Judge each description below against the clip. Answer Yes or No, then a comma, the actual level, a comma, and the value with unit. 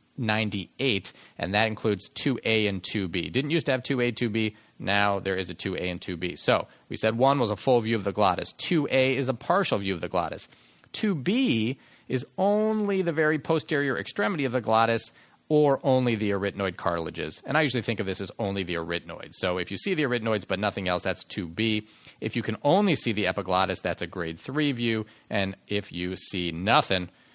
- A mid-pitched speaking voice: No, low, 110 Hz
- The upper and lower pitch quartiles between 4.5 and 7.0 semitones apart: Yes, wide, 5.6 semitones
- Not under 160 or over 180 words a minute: No, average, 200 wpm